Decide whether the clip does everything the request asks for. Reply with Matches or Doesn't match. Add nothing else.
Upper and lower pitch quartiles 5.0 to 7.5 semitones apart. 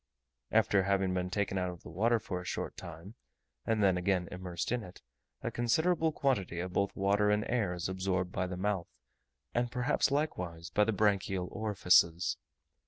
Doesn't match